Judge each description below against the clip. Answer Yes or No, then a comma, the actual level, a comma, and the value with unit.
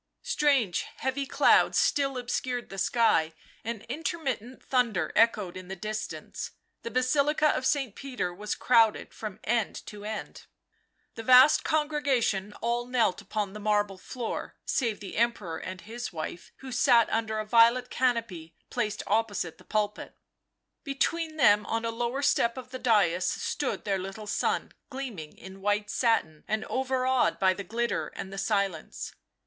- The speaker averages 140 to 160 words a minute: Yes, average, 155 wpm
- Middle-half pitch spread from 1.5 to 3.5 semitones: No, average, 4.0 semitones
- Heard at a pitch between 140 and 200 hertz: No, high, 225 Hz